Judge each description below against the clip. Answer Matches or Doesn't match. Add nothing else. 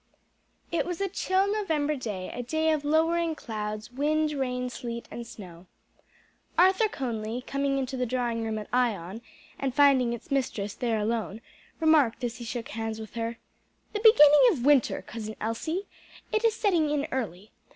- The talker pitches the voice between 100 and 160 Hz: Doesn't match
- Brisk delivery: Doesn't match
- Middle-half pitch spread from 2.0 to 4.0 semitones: Doesn't match